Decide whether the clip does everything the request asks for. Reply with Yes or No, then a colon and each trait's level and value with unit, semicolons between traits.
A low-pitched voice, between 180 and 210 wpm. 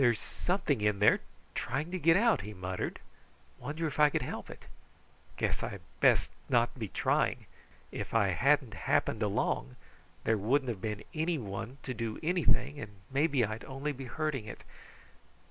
No: low, 125 Hz; average, 165 wpm